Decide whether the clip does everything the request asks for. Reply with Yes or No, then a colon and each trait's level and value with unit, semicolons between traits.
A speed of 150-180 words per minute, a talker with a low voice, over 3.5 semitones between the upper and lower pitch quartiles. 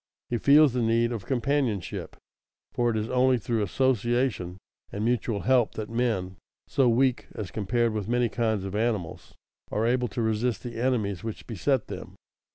No: average, 165 wpm; low, 115 Hz; average, 2.7 semitones